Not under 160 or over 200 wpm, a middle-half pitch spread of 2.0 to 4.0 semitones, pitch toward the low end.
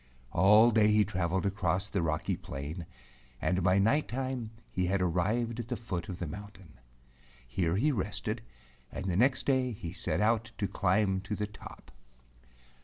Yes: average, 170 wpm; average, 3.5 semitones; low, 100 Hz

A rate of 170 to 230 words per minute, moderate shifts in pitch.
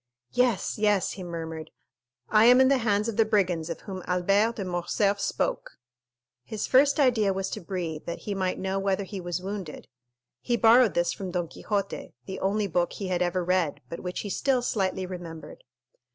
Yes: average, 190 wpm; average, 3.2 semitones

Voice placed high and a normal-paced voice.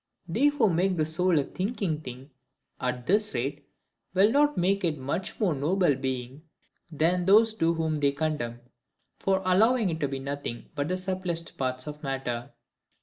No: medium, 160 Hz; average, 175 wpm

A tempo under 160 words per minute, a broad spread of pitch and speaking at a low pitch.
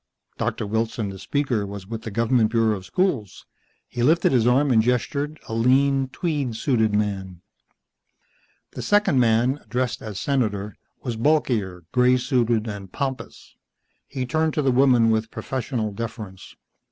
No: average, 150 wpm; average, 3.7 semitones; low, 120 Hz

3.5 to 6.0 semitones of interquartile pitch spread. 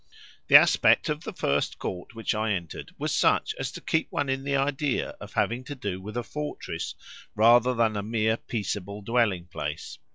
Yes: average, 4.8 semitones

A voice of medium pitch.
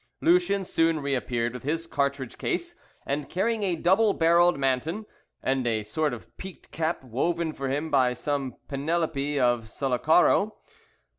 Yes: medium, 145 Hz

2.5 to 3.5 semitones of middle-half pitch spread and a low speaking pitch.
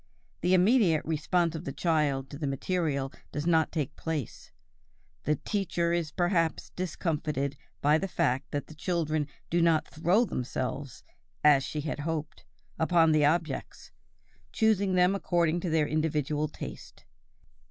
No: average, 2.8 semitones; medium, 160 Hz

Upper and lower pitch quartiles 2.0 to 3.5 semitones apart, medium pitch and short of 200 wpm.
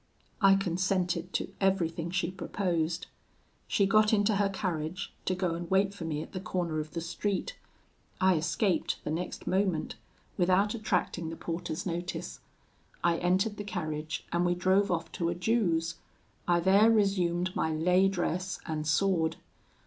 Yes: narrow, 2.6 semitones; medium, 180 Hz; average, 155 wpm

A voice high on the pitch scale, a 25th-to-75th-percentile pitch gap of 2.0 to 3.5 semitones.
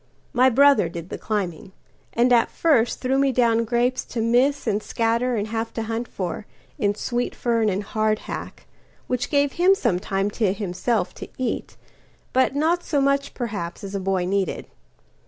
No: high, 230 Hz; average, 4.0 semitones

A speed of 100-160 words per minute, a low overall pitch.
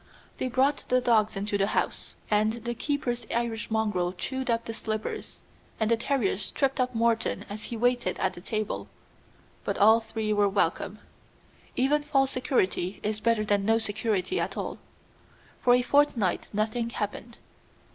No: average, 155 wpm; high, 225 Hz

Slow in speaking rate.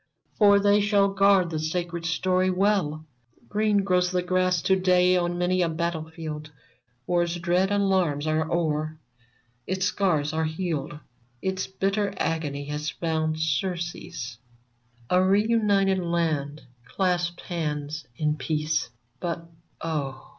Yes: slow, 130 wpm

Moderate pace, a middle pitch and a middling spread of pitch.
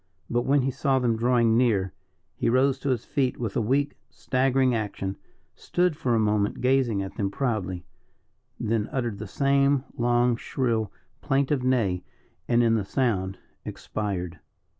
No: average, 155 wpm; low, 120 Hz; average, 4.0 semitones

